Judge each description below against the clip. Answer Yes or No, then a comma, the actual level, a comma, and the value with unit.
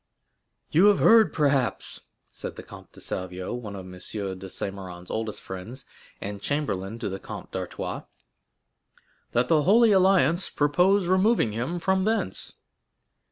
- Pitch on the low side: Yes, low, 125 Hz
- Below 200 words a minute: Yes, average, 145 wpm